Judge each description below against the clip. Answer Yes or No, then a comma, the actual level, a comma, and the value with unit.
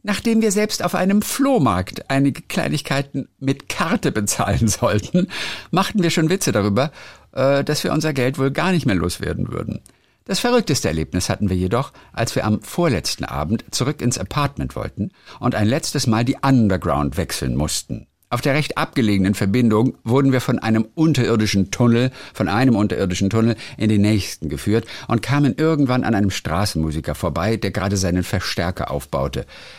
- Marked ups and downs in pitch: Yes, wide, 6.0 semitones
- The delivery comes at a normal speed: Yes, average, 165 wpm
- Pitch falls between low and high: No, low, 115 Hz